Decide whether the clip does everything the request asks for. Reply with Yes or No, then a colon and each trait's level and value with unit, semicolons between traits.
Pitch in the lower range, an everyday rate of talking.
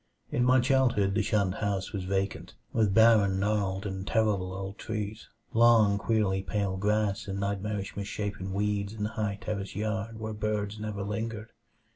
Yes: low, 105 Hz; average, 160 wpm